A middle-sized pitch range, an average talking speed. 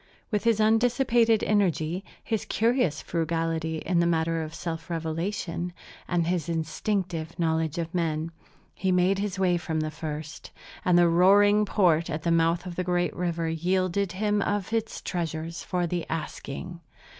Yes: average, 3.1 semitones; average, 155 wpm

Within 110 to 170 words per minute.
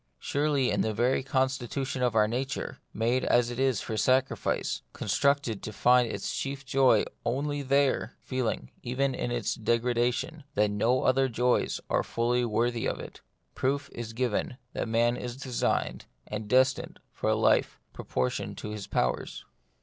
Yes: average, 155 wpm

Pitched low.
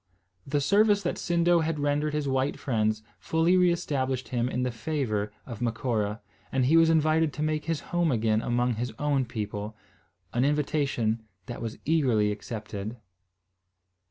Yes: low, 130 Hz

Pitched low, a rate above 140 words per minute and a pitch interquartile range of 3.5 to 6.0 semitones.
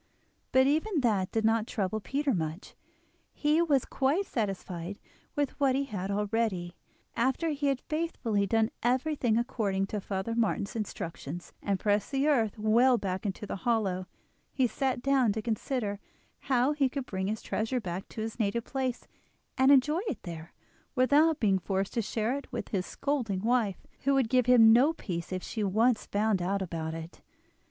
No: high, 225 Hz; average, 175 wpm; average, 5.0 semitones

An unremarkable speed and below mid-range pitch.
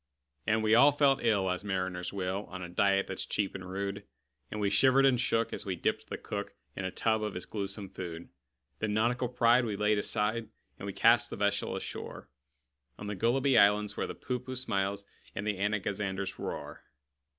Yes: average, 195 wpm; low, 105 Hz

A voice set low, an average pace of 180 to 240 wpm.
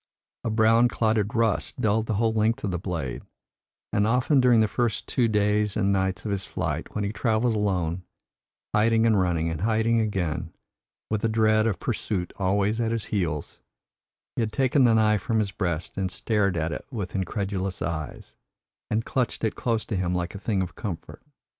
Yes: low, 105 Hz; average, 190 wpm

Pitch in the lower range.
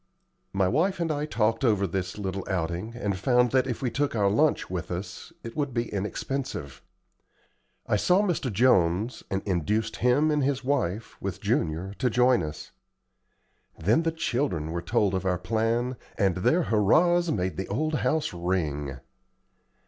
Yes: low, 110 Hz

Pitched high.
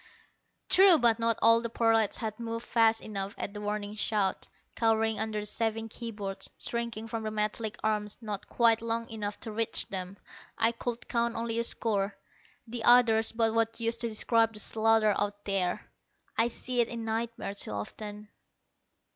Yes: high, 225 Hz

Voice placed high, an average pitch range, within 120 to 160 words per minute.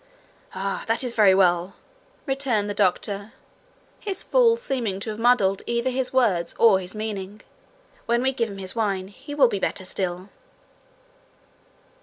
Yes: high, 215 Hz; average, 4.4 semitones; average, 155 wpm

